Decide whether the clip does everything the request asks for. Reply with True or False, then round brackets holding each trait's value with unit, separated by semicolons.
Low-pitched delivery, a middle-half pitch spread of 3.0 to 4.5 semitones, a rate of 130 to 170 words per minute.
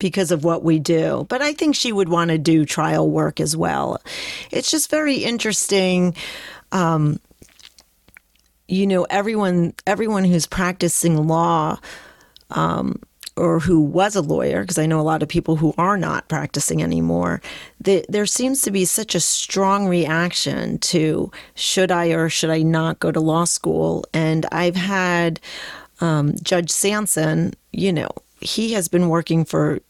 False (170 Hz; 3.3 semitones; 160 wpm)